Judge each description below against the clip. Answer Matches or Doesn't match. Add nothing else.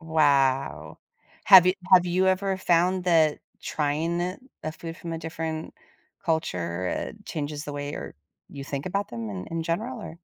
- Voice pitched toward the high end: Doesn't match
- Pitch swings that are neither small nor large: Matches